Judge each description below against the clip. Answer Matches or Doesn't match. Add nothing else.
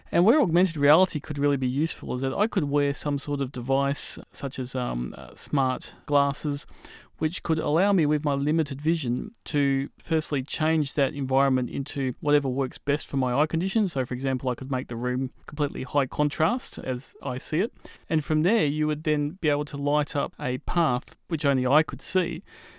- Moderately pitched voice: Matches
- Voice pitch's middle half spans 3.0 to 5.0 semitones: Doesn't match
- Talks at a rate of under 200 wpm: Doesn't match